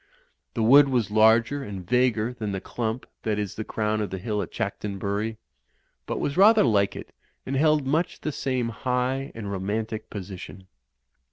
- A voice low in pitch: Yes, low, 110 Hz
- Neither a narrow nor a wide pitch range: Yes, average, 4.0 semitones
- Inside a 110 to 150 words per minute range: No, average, 175 wpm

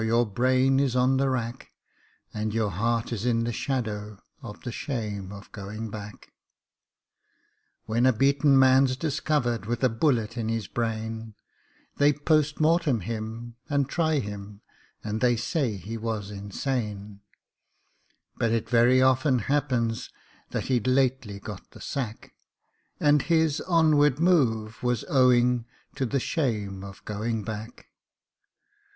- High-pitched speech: No, low, 120 Hz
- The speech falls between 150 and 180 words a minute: No, slow, 135 wpm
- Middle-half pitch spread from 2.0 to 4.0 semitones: Yes, average, 3.6 semitones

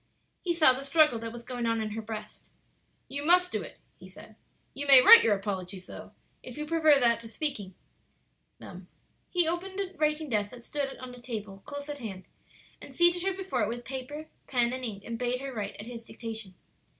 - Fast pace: Yes, fast, 210 wpm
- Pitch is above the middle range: Yes, very high, 250 Hz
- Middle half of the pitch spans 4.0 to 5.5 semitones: Yes, average, 5.2 semitones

